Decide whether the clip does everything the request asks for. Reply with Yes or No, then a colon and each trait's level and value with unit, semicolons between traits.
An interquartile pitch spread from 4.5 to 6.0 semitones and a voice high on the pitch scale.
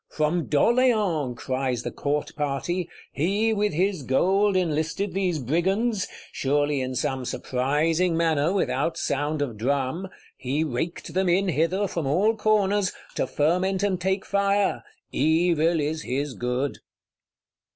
No: average, 5.1 semitones; medium, 165 Hz